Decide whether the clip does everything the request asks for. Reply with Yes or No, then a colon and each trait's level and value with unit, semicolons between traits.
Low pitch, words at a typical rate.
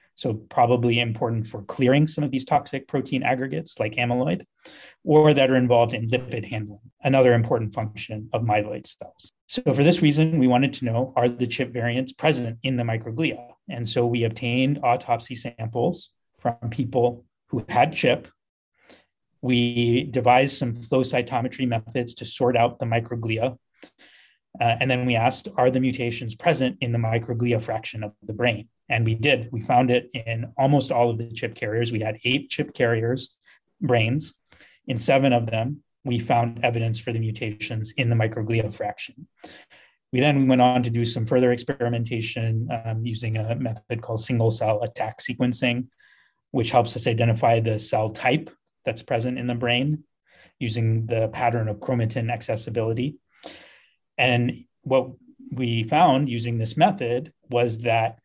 Yes: low, 120 Hz; average, 165 wpm